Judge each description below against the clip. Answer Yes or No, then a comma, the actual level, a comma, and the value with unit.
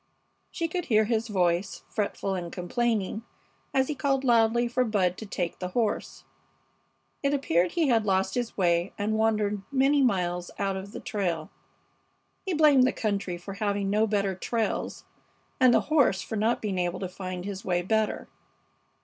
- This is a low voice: No, high, 210 Hz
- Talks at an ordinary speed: Yes, average, 170 wpm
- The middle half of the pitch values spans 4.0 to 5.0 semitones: Yes, average, 4.4 semitones